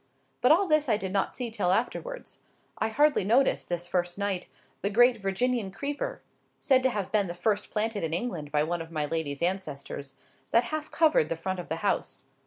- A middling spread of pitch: No, wide, 6.1 semitones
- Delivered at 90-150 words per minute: No, average, 200 wpm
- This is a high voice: Yes, high, 200 Hz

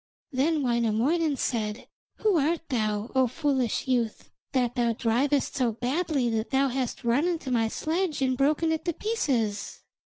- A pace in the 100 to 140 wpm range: No, average, 155 wpm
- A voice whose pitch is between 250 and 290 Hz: Yes, very high, 260 Hz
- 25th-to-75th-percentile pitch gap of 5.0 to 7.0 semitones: No, average, 4.6 semitones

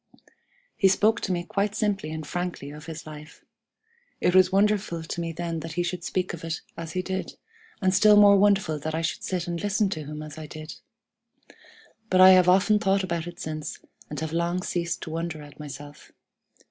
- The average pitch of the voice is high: No, medium, 170 Hz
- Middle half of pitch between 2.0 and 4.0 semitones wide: Yes, average, 3.3 semitones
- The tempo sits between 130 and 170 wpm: No, fast, 205 wpm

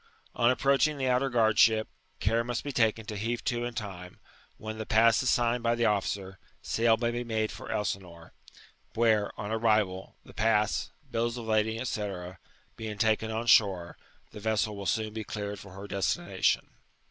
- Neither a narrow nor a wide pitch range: No, narrow, 2.3 semitones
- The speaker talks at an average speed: Yes, average, 180 wpm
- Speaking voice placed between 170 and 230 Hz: No, low, 110 Hz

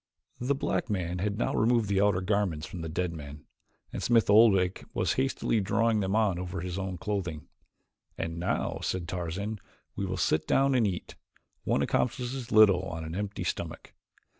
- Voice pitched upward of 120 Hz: No, very low, 95 Hz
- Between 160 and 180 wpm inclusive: Yes, average, 175 wpm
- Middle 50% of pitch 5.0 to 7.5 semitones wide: No, average, 3.7 semitones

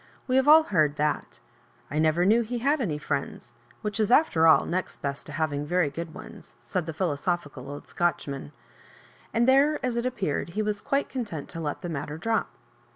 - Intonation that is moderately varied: No, wide, 7.4 semitones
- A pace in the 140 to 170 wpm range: No, average, 200 wpm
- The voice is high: No, medium, 175 Hz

